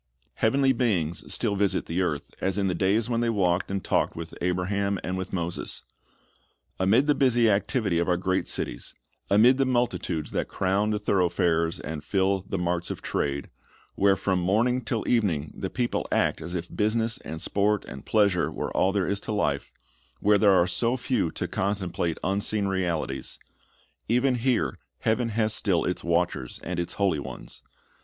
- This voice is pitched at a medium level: No, very low, 95 Hz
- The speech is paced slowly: No, average, 180 wpm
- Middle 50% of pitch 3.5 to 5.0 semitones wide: Yes, average, 3.8 semitones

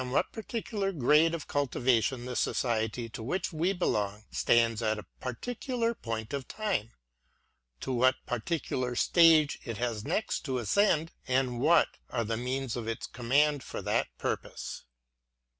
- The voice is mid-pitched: No, low, 130 Hz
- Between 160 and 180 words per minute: No, average, 150 wpm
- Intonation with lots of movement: Yes, wide, 5.9 semitones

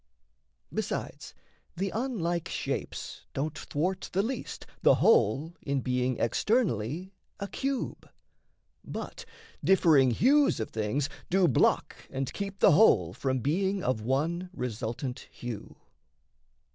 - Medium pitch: Yes, medium, 155 Hz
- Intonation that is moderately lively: No, wide, 7.5 semitones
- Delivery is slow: Yes, slow, 115 wpm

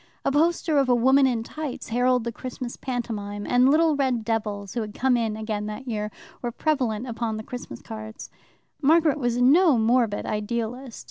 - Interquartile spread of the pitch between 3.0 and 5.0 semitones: Yes, average, 3.3 semitones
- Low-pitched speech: No, high, 240 Hz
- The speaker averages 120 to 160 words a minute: No, average, 180 wpm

